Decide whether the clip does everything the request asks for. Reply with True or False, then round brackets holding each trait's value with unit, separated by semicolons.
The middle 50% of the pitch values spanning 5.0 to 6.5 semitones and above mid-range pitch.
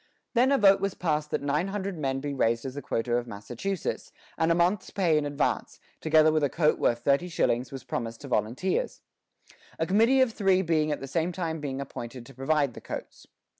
False (5.5 semitones; 155 Hz)